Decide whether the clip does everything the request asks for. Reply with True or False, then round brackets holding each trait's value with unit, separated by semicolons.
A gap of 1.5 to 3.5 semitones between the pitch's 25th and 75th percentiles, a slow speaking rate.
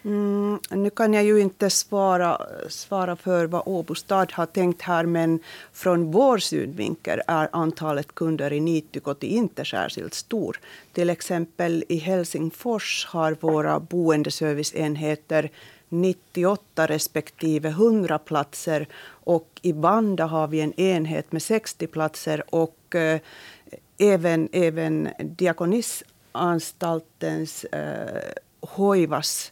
True (2.9 semitones; 110 wpm)